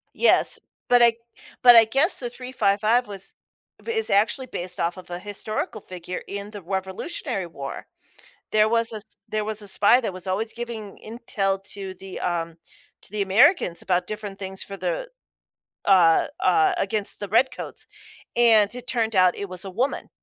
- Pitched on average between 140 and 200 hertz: No, high, 210 Hz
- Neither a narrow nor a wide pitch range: Yes, average, 3.7 semitones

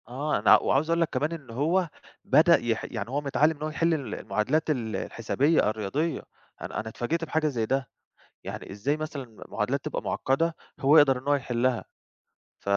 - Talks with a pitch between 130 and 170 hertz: Yes, medium, 140 Hz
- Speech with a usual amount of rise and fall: Yes, average, 4.6 semitones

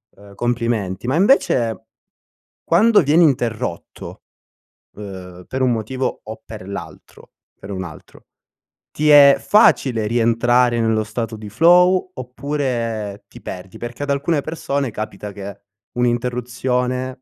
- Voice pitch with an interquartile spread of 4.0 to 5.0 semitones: Yes, average, 4.3 semitones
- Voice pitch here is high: No, low, 120 Hz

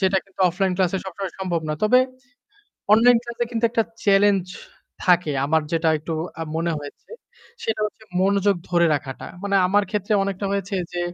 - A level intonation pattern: No, average, 3.0 semitones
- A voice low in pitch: No, high, 195 Hz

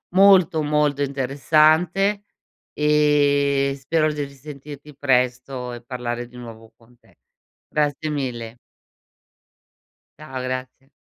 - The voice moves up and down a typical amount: Yes, average, 3.0 semitones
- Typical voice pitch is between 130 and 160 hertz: Yes, medium, 140 Hz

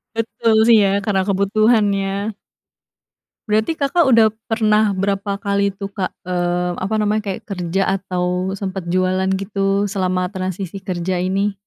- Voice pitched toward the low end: No, high, 195 Hz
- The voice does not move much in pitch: Yes, narrow, 2.3 semitones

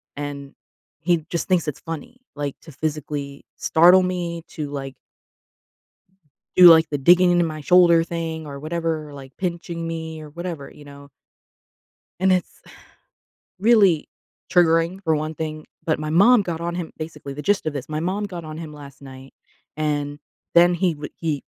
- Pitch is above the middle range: No, medium, 160 Hz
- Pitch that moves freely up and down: No, average, 2.8 semitones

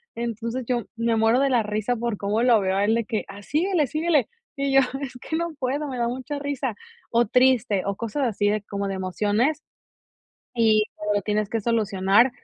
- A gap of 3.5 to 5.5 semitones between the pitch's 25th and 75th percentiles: Yes, average, 4.0 semitones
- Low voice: No, high, 230 Hz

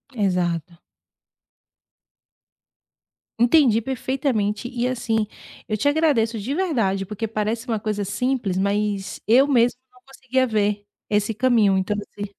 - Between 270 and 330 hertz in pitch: No, high, 220 Hz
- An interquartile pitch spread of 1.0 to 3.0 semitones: No, average, 3.6 semitones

